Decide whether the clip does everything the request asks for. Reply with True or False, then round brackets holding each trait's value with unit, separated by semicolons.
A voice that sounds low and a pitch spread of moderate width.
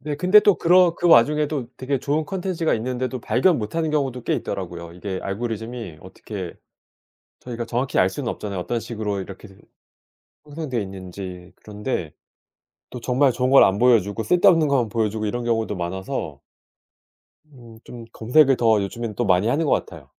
False (120 Hz; 5.7 semitones)